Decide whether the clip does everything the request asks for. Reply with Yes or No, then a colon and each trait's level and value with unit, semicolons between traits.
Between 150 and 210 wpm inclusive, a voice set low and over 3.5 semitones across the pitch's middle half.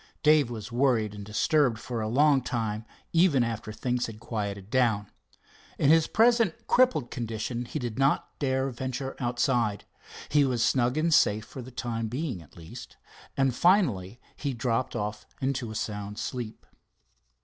Yes: average, 160 wpm; low, 120 Hz; average, 3.9 semitones